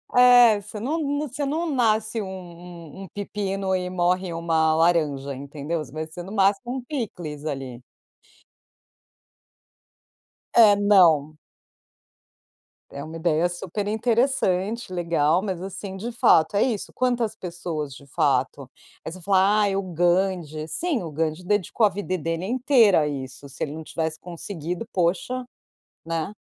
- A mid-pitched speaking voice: Yes, medium, 180 Hz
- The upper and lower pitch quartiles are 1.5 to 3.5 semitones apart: No, average, 4.8 semitones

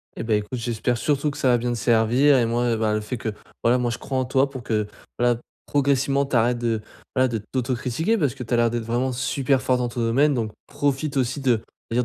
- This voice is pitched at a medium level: No, low, 125 Hz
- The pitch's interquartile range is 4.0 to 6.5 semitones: No, narrow, 2.5 semitones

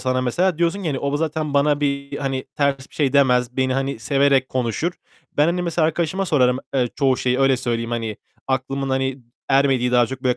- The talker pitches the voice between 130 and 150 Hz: Yes, low, 135 Hz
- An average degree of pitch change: No, narrow, 2.3 semitones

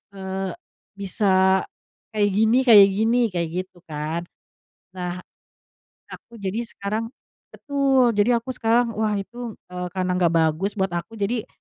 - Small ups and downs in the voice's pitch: No, average, 3.9 semitones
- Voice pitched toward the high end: Yes, high, 200 Hz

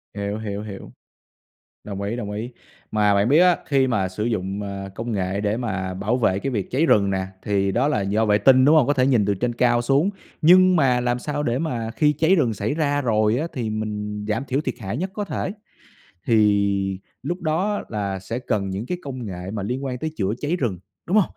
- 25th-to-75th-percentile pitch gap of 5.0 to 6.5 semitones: Yes, wide, 5.4 semitones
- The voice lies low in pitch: Yes, low, 115 Hz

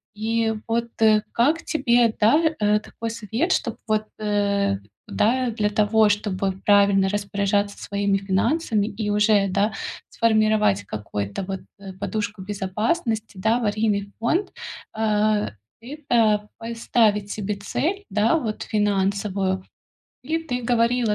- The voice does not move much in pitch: Yes, narrow, 2.3 semitones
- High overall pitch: Yes, high, 210 Hz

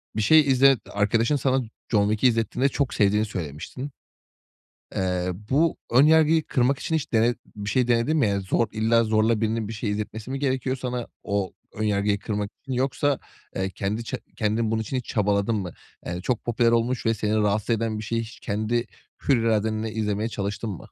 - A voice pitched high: No, low, 115 Hz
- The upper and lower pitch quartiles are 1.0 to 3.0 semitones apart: No, average, 3.4 semitones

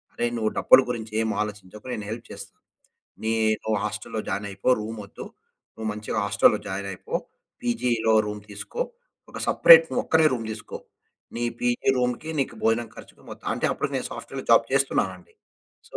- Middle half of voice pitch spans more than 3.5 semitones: No, narrow, 2.4 semitones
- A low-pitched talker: Yes, low, 110 Hz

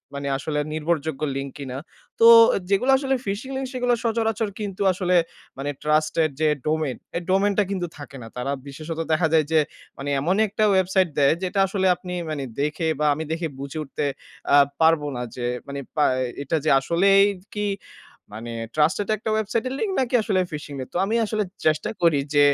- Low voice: No, medium, 165 Hz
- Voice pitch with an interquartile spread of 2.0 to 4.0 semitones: No, average, 5.3 semitones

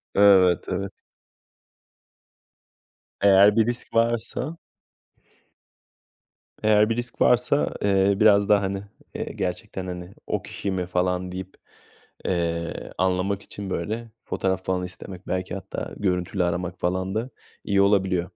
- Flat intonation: Yes, narrow, 2.1 semitones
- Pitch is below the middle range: Yes, very low, 95 Hz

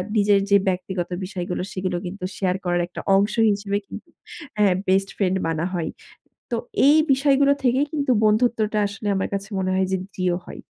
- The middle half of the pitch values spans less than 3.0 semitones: Yes, narrow, 2.6 semitones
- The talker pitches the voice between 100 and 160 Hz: No, high, 195 Hz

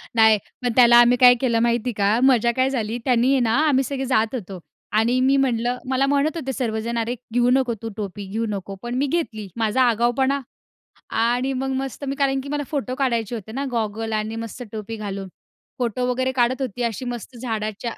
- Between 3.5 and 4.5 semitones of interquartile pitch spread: No, average, 2.8 semitones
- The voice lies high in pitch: Yes, high, 240 Hz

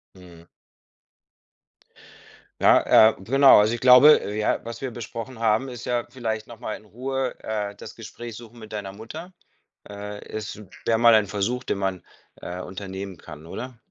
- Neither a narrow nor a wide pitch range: Yes, average, 3.1 semitones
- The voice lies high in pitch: No, low, 110 Hz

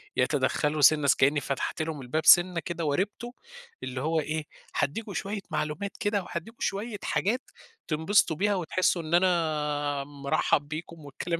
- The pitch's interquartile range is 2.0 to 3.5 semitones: No, average, 4.1 semitones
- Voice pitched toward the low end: No, medium, 160 Hz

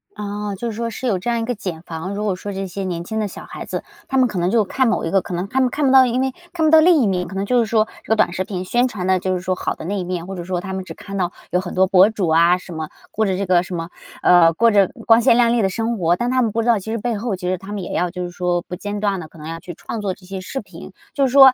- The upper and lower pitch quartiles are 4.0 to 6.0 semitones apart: Yes, average, 4.3 semitones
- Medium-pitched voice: No, high, 195 Hz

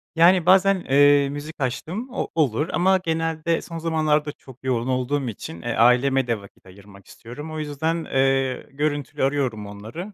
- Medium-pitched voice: Yes, medium, 145 Hz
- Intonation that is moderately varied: Yes, average, 4.4 semitones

